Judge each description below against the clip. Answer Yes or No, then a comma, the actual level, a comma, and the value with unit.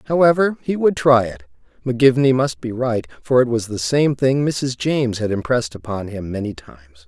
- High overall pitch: No, low, 120 Hz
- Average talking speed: Yes, average, 195 wpm